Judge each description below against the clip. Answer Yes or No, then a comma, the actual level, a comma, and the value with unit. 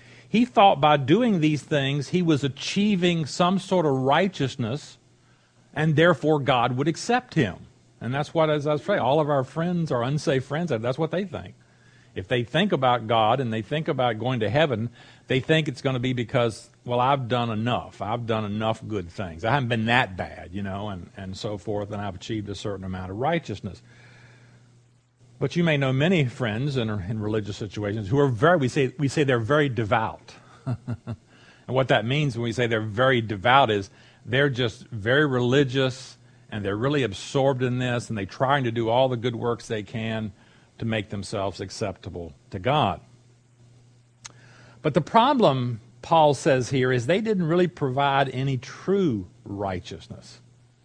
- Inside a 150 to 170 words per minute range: No, average, 185 wpm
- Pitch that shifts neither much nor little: Yes, average, 4.3 semitones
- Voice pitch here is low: Yes, low, 125 Hz